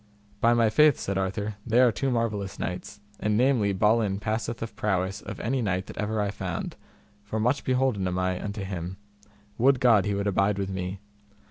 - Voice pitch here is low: Yes, low, 105 Hz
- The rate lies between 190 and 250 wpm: Yes, average, 195 wpm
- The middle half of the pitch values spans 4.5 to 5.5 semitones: No, average, 3.2 semitones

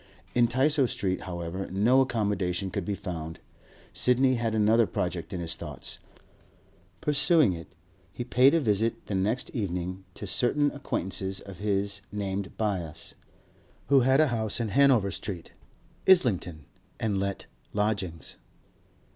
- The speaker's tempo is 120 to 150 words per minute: Yes, slow, 135 wpm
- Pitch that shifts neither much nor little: Yes, average, 4.8 semitones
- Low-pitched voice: Yes, low, 105 Hz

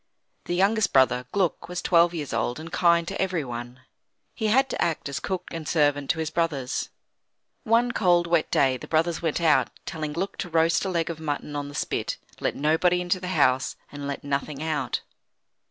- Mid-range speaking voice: Yes, medium, 160 Hz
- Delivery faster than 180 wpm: Yes, average, 195 wpm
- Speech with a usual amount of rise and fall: Yes, average, 3.7 semitones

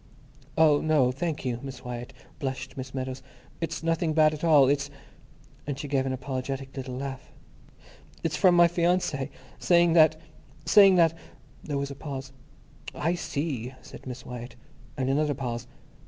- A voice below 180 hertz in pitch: Yes, medium, 140 Hz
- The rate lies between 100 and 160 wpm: Yes, average, 150 wpm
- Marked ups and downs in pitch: No, average, 3.4 semitones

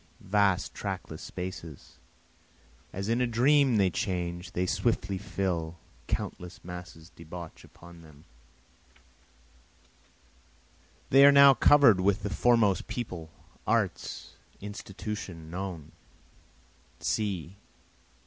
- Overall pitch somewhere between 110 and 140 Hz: No, very low, 95 Hz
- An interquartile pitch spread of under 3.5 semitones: No, average, 4.0 semitones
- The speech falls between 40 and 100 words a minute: Yes, slow, 95 wpm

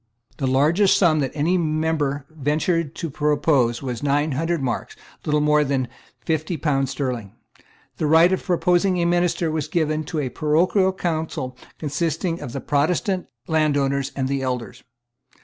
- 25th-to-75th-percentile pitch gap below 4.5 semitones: Yes, average, 3.4 semitones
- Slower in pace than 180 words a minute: Yes, average, 150 wpm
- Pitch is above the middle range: No, medium, 150 Hz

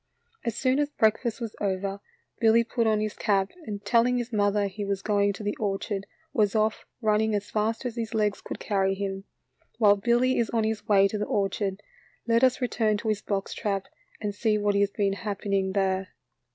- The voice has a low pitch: No, high, 210 Hz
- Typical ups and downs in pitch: No, narrow, 2.1 semitones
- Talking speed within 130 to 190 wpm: No, average, 200 wpm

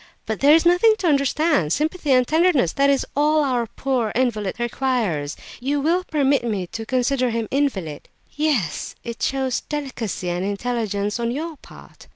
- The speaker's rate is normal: Yes, average, 180 wpm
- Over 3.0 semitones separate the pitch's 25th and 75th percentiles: Yes, average, 5.0 semitones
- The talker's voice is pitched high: Yes, very high, 255 Hz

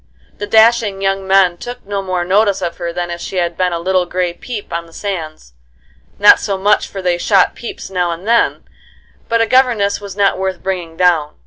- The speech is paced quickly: Yes, fast, 210 wpm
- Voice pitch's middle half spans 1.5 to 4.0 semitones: Yes, narrow, 2.6 semitones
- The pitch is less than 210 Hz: Yes, high, 190 Hz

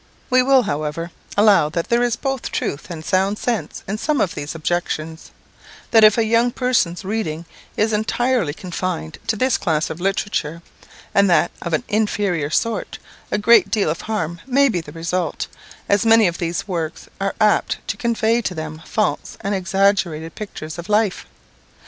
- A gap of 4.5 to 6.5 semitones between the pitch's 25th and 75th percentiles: Yes, average, 4.9 semitones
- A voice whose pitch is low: No, high, 195 Hz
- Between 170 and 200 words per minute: Yes, average, 175 wpm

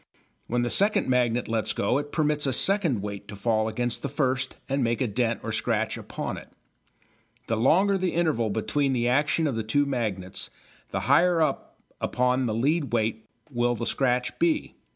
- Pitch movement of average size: Yes, average, 4.3 semitones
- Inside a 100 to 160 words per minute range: No, average, 185 wpm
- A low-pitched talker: Yes, low, 125 Hz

